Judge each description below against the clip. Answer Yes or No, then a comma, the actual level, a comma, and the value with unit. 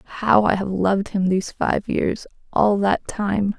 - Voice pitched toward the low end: No, high, 200 Hz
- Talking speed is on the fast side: No, average, 185 wpm